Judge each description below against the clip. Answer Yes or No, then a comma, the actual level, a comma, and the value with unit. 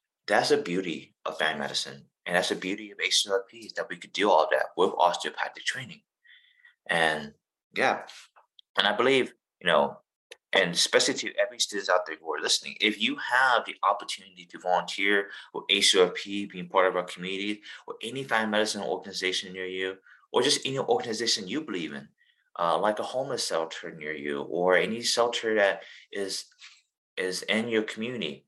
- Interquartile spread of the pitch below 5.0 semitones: Yes, average, 4.2 semitones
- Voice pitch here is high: No, low, 100 Hz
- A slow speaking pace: No, average, 175 wpm